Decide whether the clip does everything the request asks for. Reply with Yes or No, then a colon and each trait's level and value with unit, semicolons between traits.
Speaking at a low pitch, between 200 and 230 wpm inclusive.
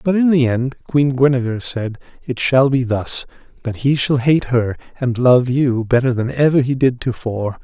Yes: low, 130 Hz; fast, 205 wpm